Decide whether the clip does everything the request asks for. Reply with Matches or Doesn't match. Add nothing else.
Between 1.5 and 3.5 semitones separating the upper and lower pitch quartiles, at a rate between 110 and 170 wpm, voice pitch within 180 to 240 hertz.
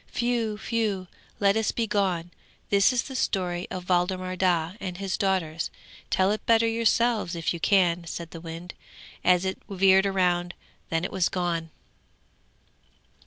Matches